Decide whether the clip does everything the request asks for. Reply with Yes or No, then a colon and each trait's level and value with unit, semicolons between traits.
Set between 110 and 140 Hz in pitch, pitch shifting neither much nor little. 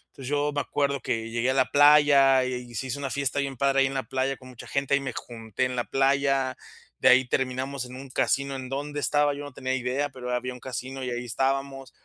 No: low, 135 Hz; narrow, 1.5 semitones